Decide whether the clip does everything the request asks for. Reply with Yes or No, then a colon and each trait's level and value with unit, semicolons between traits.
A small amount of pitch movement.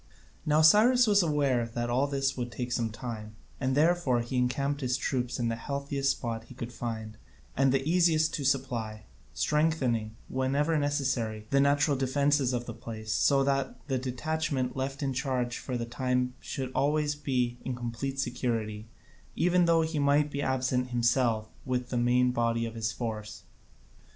No: average, 3.0 semitones